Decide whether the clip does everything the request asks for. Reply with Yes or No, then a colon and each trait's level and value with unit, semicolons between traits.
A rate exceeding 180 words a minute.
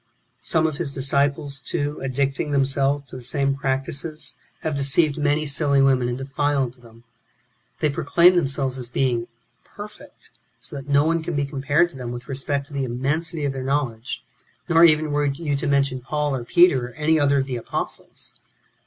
Yes: average, 190 wpm